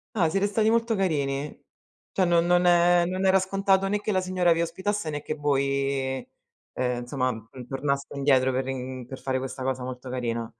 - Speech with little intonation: No, wide, 6.0 semitones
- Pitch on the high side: No, medium, 145 Hz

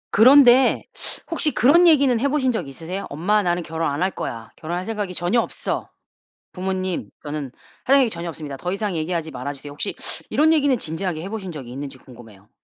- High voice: No, medium, 180 Hz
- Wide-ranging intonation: Yes, wide, 7.3 semitones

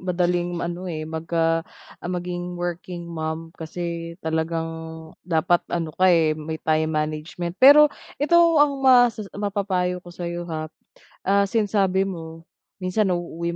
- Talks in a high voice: No, medium, 175 Hz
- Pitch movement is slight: Yes, narrow, 2.3 semitones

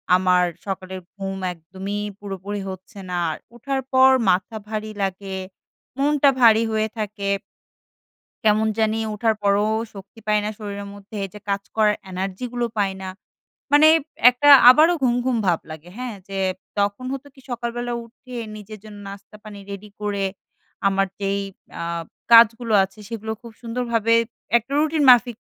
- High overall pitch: Yes, high, 215 Hz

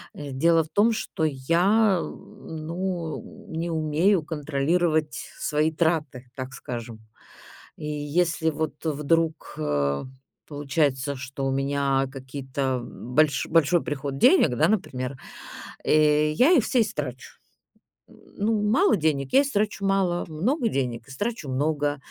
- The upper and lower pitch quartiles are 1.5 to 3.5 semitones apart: No, average, 4.2 semitones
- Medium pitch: Yes, medium, 155 Hz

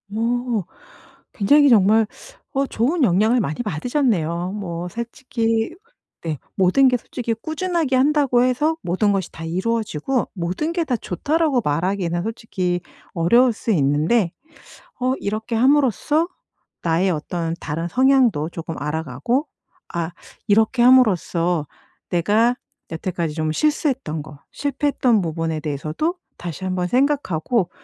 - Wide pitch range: Yes, wide, 7.0 semitones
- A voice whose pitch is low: No, high, 215 Hz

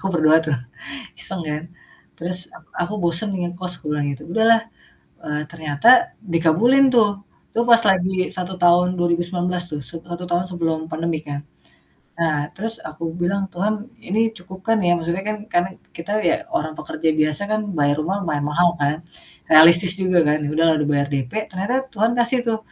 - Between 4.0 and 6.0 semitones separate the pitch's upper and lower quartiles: No, average, 3.4 semitones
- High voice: No, medium, 175 Hz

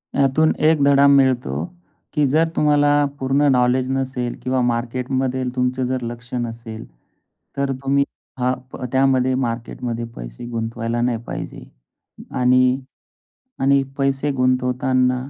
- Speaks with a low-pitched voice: Yes, low, 130 Hz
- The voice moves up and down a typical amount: No, narrow, 1.8 semitones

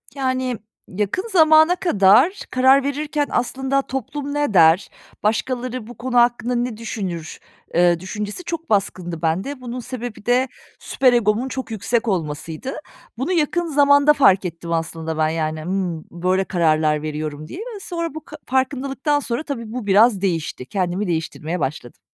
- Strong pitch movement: Yes, wide, 7.6 semitones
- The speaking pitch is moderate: No, high, 230 Hz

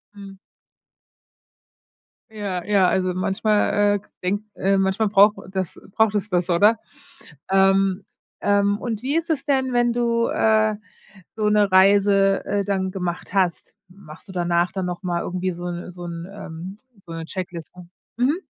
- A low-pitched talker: No, high, 195 Hz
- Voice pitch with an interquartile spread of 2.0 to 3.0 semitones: Yes, narrow, 2.6 semitones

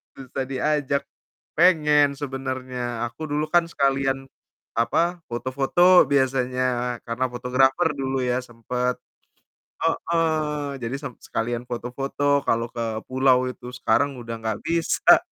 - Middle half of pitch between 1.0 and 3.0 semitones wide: Yes, narrow, 2.6 semitones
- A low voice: Yes, low, 130 Hz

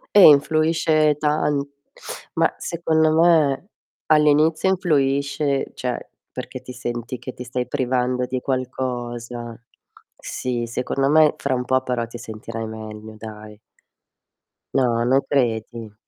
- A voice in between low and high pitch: No, low, 130 Hz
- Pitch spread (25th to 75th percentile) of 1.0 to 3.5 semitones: No, average, 3.9 semitones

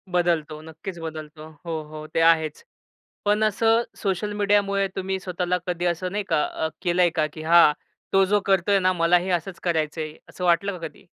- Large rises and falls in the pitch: No, average, 3.2 semitones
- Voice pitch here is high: No, medium, 175 Hz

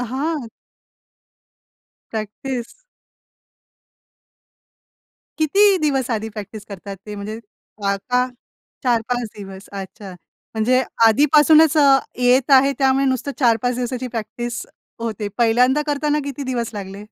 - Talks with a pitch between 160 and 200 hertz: No, high, 245 Hz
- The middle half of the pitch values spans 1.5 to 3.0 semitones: No, average, 4.0 semitones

